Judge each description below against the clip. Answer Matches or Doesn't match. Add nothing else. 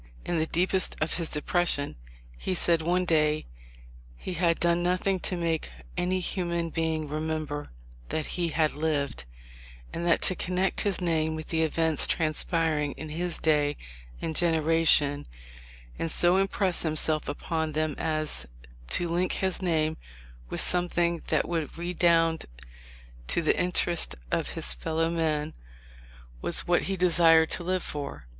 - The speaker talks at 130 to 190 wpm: Matches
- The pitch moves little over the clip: Matches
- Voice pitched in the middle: Matches